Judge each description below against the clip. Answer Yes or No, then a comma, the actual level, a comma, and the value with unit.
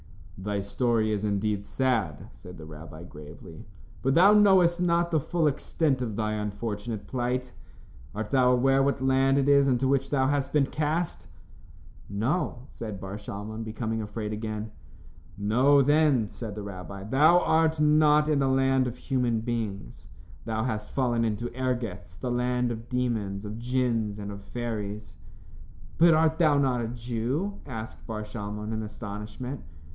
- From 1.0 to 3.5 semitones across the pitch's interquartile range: No, average, 4.3 semitones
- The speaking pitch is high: No, low, 120 Hz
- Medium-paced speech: Yes, average, 160 wpm